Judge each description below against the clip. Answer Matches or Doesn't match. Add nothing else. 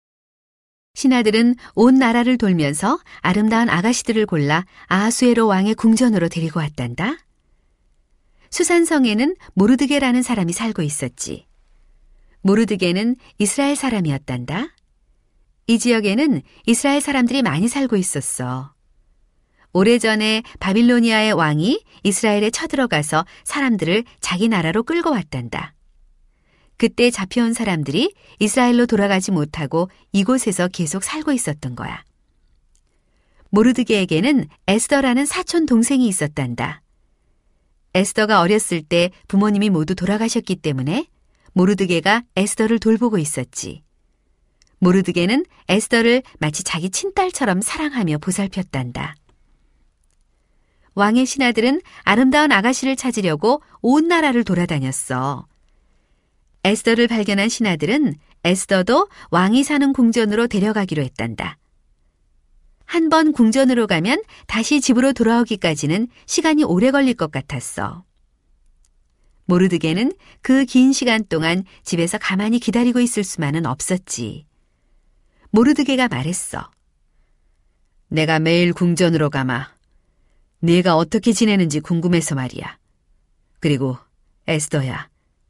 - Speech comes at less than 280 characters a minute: Doesn't match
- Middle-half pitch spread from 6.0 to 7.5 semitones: Doesn't match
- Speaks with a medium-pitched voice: Doesn't match